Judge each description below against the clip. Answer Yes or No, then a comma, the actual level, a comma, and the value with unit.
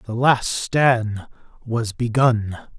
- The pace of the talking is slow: Yes, slow, 110 wpm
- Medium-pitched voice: No, low, 115 Hz